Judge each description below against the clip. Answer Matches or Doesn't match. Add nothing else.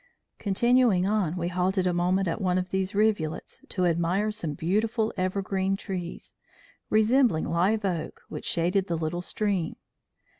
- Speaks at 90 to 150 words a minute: Matches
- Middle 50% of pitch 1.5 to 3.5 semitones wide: Matches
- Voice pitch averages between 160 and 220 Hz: Matches